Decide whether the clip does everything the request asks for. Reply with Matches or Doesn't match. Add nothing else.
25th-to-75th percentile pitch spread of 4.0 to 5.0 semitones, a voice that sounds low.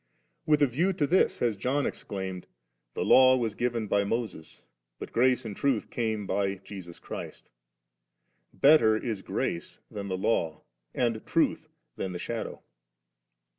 Matches